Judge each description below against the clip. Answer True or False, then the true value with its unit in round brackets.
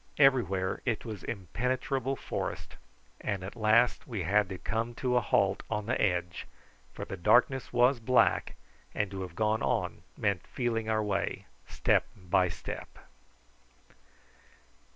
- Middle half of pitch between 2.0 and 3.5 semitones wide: False (4.0 semitones)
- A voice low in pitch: True (110 Hz)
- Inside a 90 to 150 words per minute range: True (140 wpm)